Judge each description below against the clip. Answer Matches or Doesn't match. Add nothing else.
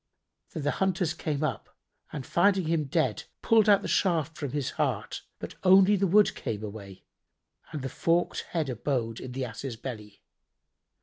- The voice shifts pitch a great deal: Matches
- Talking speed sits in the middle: Matches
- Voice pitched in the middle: Matches